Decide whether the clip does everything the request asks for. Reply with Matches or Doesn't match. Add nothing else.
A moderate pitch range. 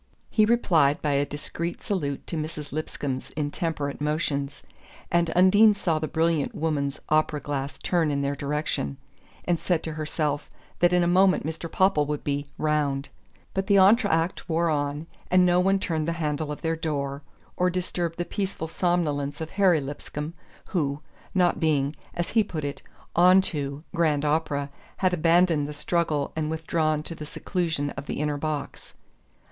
Matches